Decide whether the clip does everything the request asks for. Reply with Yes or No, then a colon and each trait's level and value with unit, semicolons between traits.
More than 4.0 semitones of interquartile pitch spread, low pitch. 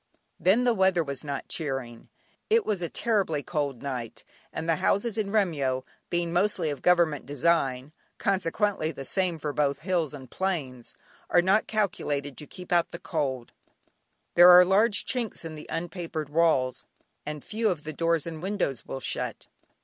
No: average, 4.9 semitones; medium, 165 Hz